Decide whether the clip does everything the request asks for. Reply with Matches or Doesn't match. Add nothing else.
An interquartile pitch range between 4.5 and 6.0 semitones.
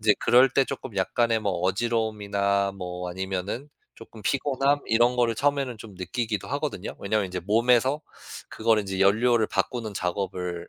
Doesn't match